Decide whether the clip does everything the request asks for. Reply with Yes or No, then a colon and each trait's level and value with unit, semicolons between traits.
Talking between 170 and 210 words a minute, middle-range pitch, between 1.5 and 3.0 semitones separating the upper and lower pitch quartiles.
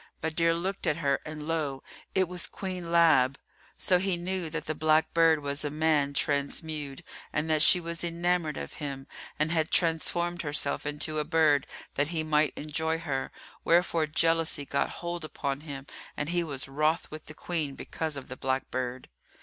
Yes: average, 180 wpm; medium, 155 Hz; narrow, 2.6 semitones